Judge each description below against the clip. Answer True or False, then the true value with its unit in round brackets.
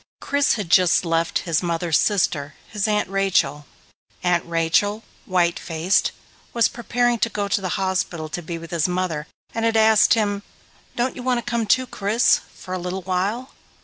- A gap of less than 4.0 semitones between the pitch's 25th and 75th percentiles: False (4.5 semitones)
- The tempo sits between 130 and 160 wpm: False (180 wpm)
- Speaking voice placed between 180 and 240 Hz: True (190 Hz)